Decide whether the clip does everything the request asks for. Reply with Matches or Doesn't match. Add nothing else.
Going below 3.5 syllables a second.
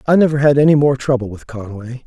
Doesn't match